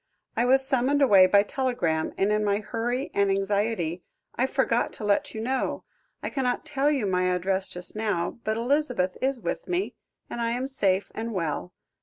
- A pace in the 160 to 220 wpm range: Yes, average, 185 wpm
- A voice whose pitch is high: Yes, high, 220 Hz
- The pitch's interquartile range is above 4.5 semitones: Yes, average, 5.2 semitones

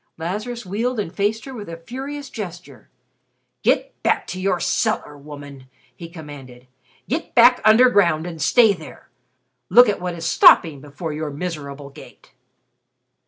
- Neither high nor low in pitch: Yes, medium, 175 Hz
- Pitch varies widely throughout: Yes, wide, 6.5 semitones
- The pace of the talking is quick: No, average, 150 wpm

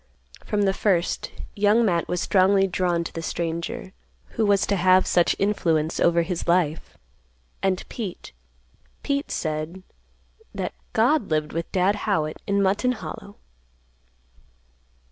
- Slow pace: Yes, slow, 125 wpm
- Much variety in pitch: No, average, 3.4 semitones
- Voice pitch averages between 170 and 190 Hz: Yes, medium, 185 Hz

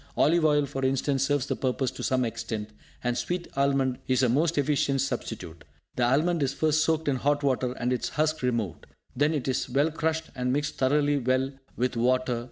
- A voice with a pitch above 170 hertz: No, low, 135 Hz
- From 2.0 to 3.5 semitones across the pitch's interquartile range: Yes, average, 2.7 semitones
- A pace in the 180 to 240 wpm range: Yes, average, 195 wpm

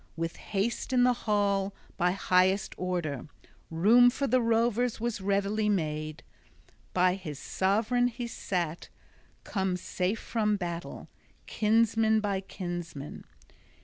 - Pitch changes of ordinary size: Yes, average, 3.8 semitones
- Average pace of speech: No, slow, 115 wpm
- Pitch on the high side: Yes, high, 200 Hz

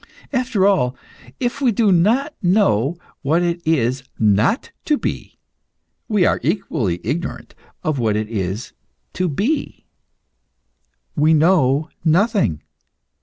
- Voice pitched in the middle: Yes, medium, 165 Hz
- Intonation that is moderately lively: No, wide, 8.4 semitones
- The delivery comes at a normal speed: No, slow, 115 wpm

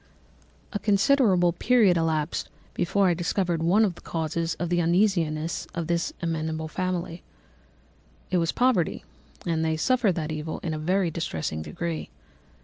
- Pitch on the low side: No, medium, 170 Hz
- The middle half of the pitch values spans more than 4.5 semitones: No, narrow, 2.6 semitones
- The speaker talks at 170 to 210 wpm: No, average, 145 wpm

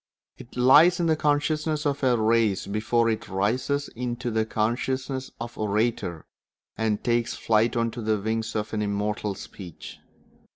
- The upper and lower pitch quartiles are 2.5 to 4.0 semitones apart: Yes, average, 3.4 semitones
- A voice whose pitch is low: Yes, low, 115 Hz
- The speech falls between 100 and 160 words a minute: Yes, average, 150 wpm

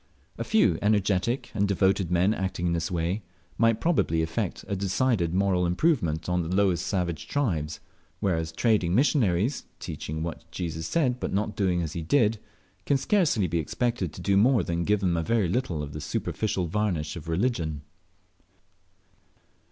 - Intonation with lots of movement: No, average, 4.6 semitones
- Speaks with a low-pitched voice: Yes, very low, 95 Hz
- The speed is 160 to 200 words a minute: Yes, average, 165 wpm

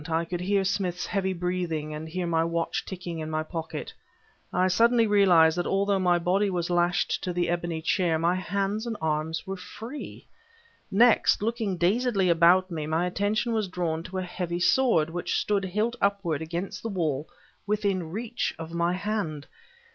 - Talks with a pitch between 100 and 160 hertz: No, medium, 180 Hz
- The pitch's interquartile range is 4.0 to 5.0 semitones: No, average, 3.2 semitones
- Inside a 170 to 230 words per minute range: Yes, average, 175 wpm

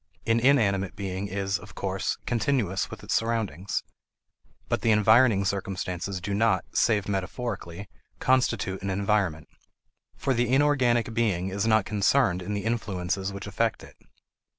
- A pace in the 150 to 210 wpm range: No, average, 140 wpm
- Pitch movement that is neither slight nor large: Yes, average, 3.2 semitones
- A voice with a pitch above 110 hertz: No, low, 100 Hz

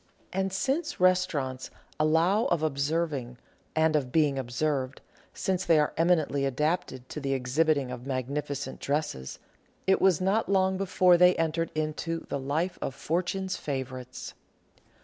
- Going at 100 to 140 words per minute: Yes, slow, 135 wpm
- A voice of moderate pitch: Yes, medium, 155 Hz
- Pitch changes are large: No, average, 4.8 semitones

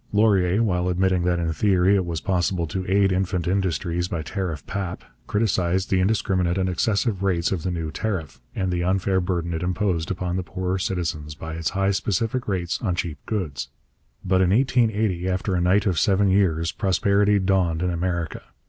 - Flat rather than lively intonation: Yes, narrow, 2.1 semitones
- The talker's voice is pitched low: Yes, very low, 95 Hz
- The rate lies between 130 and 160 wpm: No, average, 185 wpm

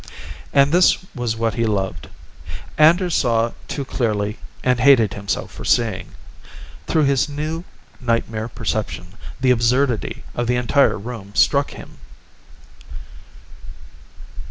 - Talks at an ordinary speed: No, slow, 115 wpm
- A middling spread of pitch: Yes, average, 4.1 semitones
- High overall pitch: No, low, 120 Hz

